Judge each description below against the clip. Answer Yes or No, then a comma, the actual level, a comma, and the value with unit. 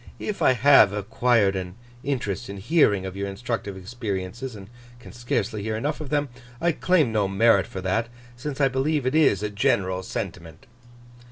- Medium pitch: No, low, 115 Hz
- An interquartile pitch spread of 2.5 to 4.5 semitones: No, average, 5.3 semitones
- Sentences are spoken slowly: No, average, 175 wpm